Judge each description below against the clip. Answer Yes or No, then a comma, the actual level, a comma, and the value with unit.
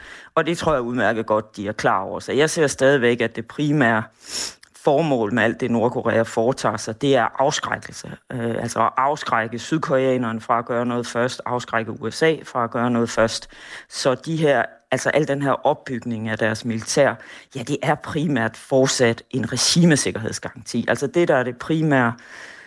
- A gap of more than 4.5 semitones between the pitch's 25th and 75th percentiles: No, average, 3.3 semitones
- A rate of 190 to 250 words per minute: No, average, 175 wpm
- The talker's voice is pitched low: Yes, low, 120 Hz